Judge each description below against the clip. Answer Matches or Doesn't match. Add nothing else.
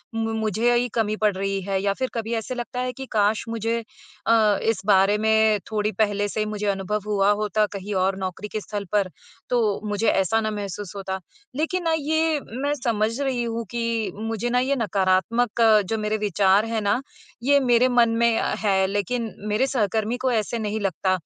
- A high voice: Matches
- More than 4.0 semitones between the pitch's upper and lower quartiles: Doesn't match